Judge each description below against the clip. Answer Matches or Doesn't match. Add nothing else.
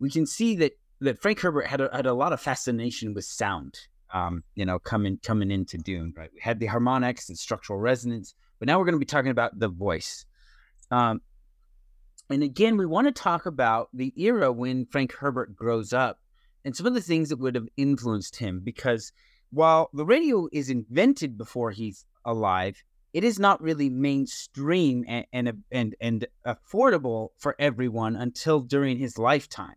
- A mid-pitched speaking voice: Doesn't match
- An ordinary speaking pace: Matches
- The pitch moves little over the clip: Doesn't match